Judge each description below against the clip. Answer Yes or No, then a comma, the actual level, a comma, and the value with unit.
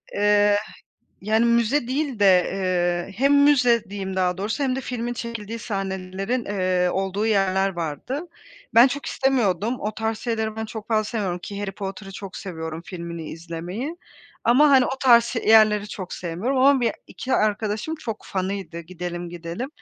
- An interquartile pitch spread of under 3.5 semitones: No, average, 4.1 semitones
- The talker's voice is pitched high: Yes, high, 210 Hz